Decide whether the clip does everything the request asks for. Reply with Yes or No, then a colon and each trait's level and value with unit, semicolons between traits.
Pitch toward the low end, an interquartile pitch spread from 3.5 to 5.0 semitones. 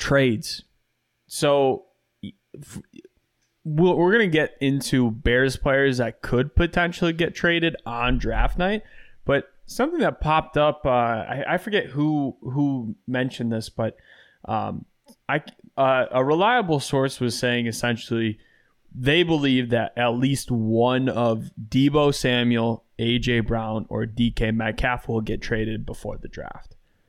Yes: low, 125 Hz; average, 3.9 semitones